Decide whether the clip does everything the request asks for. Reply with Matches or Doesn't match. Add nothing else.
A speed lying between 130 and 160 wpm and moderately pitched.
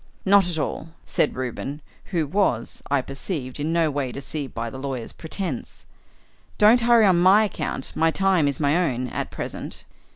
Doesn't match